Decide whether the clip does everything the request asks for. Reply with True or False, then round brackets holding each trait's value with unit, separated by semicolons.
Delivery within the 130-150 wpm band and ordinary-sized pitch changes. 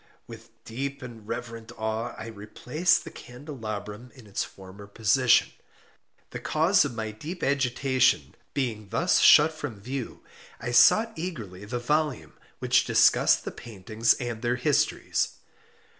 True (135 wpm; 3.8 semitones)